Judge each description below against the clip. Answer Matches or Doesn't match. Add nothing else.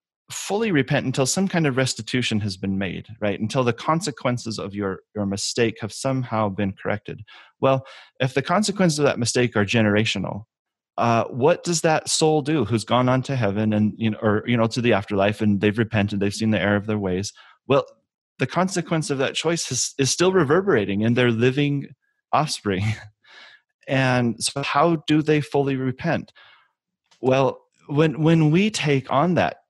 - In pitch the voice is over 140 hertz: Doesn't match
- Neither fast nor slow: Matches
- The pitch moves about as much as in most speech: Doesn't match